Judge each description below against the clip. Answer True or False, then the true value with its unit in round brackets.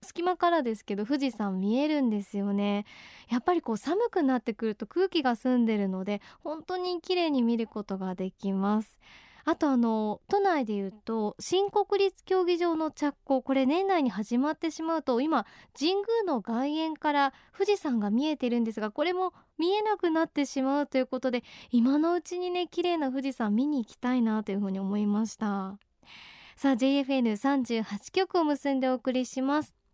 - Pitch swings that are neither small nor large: False (6.8 semitones)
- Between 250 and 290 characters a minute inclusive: False (355 characters per minute)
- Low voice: False (270 Hz)